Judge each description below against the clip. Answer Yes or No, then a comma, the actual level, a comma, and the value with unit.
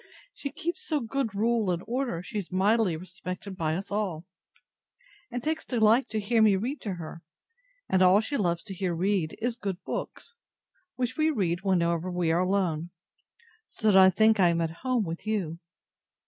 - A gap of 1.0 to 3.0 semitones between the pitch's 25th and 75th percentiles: No, average, 4.7 semitones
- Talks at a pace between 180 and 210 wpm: Yes, average, 185 wpm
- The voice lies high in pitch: Yes, high, 195 Hz